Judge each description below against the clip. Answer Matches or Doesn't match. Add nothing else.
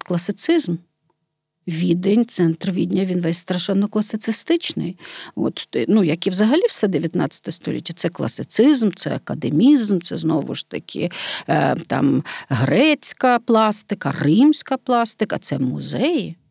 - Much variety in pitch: Matches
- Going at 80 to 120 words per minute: Matches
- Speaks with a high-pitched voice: Matches